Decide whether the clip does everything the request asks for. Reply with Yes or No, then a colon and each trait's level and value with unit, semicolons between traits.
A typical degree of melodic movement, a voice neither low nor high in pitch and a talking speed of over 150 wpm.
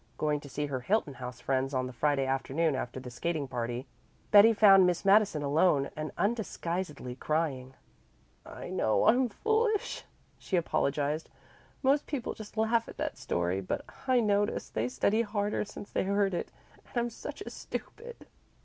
No: wide, 7.9 semitones; medium, 165 Hz; average, 165 wpm